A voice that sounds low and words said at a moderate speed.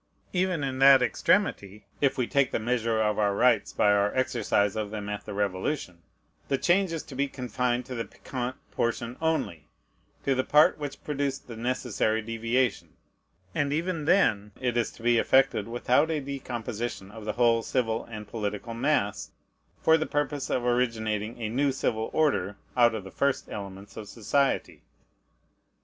Yes: low, 120 Hz; average, 170 wpm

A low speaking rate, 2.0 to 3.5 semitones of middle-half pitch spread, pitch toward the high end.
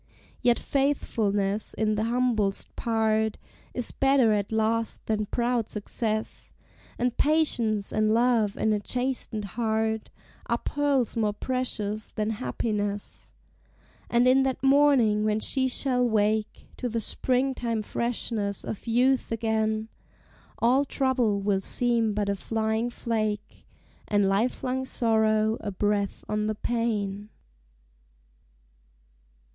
Yes: slow, 120 wpm; average, 2.7 semitones; high, 220 Hz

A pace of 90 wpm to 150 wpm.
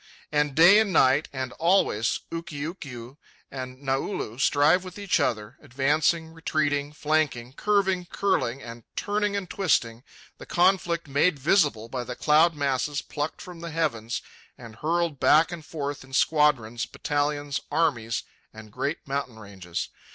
Yes: average, 140 wpm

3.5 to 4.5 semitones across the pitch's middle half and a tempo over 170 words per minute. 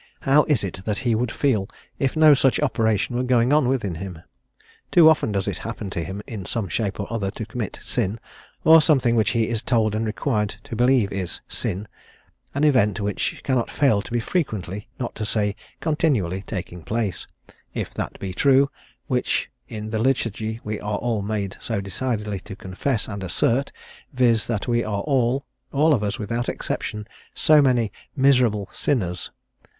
Yes: average, 4.2 semitones; average, 180 wpm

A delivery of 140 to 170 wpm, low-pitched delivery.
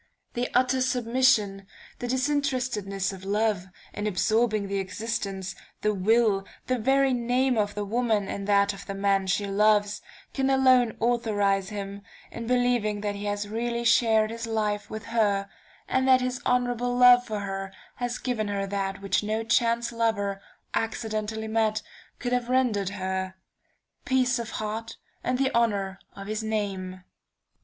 No: average, 155 wpm; high, 220 Hz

